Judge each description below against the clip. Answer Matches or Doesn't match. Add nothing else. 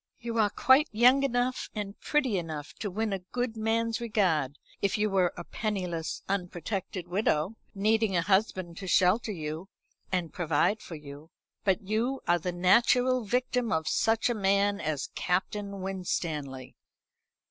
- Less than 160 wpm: Matches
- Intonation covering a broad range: Doesn't match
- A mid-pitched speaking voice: Doesn't match